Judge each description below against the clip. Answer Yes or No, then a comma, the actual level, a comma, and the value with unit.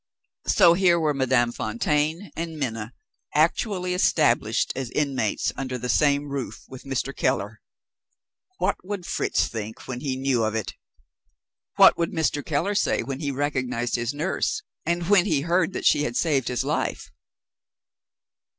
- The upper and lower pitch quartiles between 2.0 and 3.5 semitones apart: No, average, 4.9 semitones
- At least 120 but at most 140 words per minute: No, average, 150 wpm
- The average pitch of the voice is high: No, medium, 140 Hz